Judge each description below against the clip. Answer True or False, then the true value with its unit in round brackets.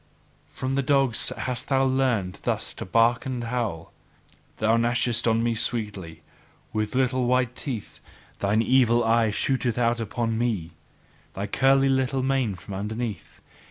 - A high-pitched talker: False (120 Hz)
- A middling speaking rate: True (145 wpm)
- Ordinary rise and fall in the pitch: True (3.1 semitones)